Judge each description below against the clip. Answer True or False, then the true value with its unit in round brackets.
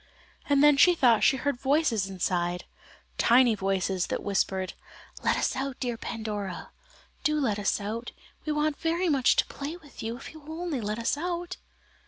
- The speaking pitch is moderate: False (250 Hz)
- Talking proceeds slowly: False (180 wpm)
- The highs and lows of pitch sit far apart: True (6.5 semitones)